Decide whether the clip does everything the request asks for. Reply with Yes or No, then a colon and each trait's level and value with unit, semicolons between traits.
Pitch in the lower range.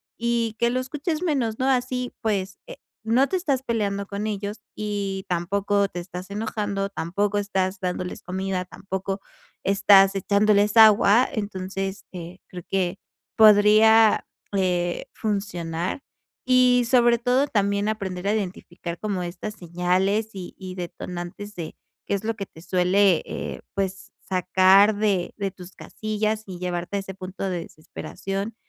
No: high, 200 Hz